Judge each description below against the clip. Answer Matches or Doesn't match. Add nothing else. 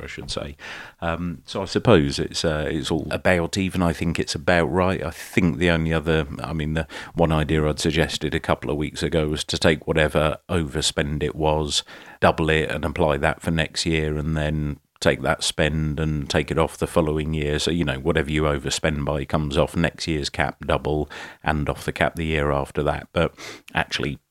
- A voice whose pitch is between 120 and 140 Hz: Doesn't match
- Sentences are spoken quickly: Matches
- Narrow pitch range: Matches